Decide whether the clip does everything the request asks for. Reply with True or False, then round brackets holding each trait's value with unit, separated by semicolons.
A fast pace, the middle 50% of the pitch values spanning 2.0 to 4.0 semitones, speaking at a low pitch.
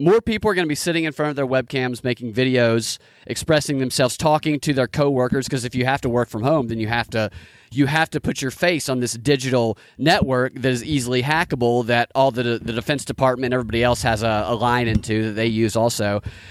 True (230 wpm; 3.4 semitones; 125 Hz)